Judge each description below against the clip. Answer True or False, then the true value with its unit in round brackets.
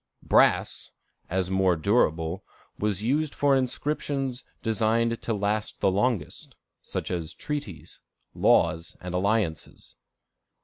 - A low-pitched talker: True (105 Hz)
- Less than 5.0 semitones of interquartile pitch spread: False (5.3 semitones)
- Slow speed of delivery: True (105 wpm)